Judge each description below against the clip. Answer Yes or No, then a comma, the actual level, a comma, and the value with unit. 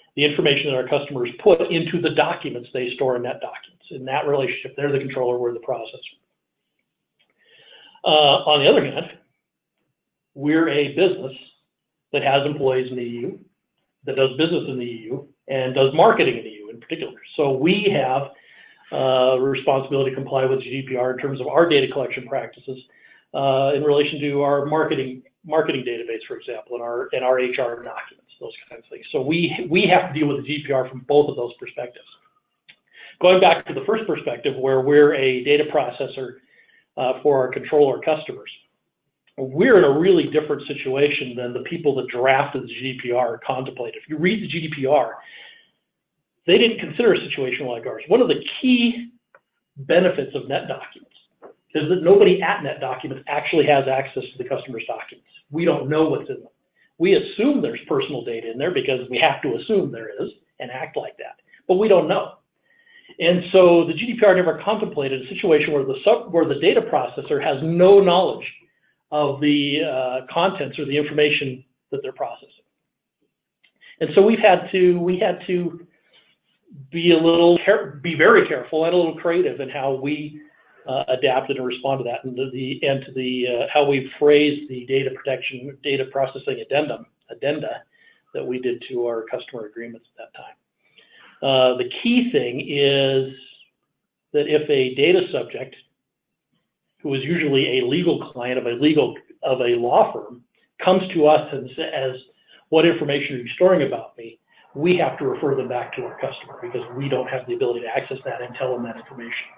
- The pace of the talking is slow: No, average, 180 wpm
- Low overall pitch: No, medium, 145 Hz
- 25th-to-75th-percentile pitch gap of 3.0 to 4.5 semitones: No, average, 5.3 semitones